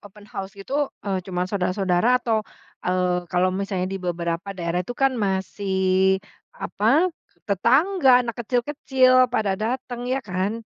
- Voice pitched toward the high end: Yes, high, 195 Hz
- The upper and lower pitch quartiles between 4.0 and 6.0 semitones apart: Yes, average, 4.6 semitones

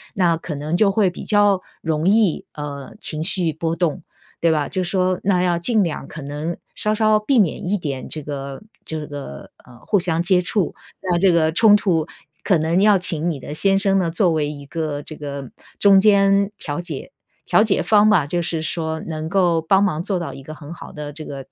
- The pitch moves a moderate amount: Yes, average, 4.2 semitones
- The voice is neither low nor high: Yes, medium, 170 Hz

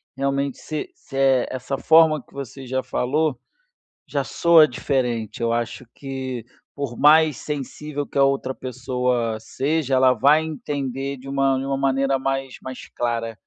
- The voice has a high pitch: No, low, 135 Hz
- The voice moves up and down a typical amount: No, narrow, 1.8 semitones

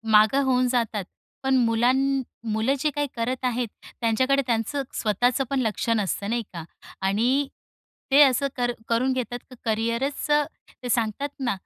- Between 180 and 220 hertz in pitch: No, high, 245 Hz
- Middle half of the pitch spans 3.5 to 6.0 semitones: No, average, 2.8 semitones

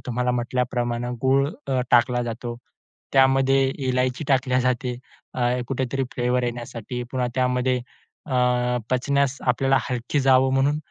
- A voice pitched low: Yes, low, 125 Hz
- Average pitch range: No, narrow, 1.4 semitones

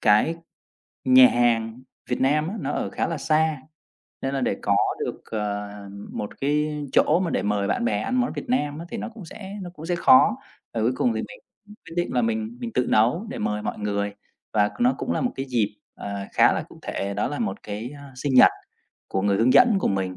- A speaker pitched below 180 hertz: Yes, low, 135 Hz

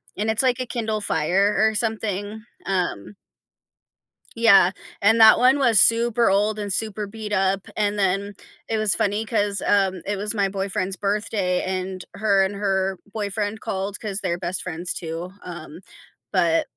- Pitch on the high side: Yes, high, 200 Hz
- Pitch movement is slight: Yes, narrow, 2.3 semitones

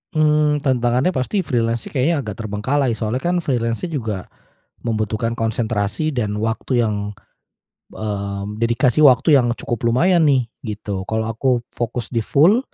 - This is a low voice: Yes, low, 120 Hz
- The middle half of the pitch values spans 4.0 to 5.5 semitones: Yes, average, 4.3 semitones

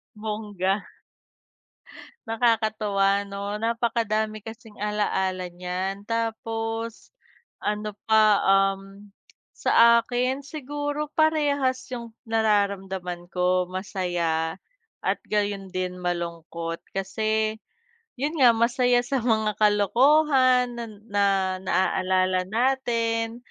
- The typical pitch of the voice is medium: No, high, 215 Hz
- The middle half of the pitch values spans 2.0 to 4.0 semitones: Yes, average, 3.4 semitones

